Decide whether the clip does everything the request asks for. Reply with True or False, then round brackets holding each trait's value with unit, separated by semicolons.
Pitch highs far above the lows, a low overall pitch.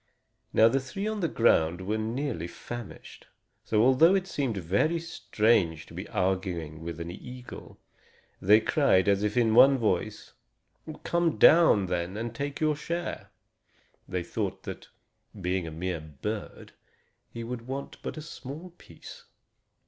True (7.2 semitones; 110 Hz)